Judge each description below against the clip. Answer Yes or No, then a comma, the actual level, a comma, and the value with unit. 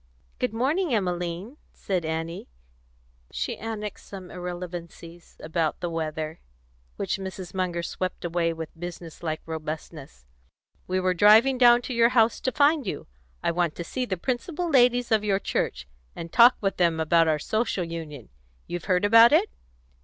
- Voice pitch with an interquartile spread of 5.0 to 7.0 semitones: Yes, wide, 5.5 semitones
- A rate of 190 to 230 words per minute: No, average, 160 wpm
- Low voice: No, medium, 180 Hz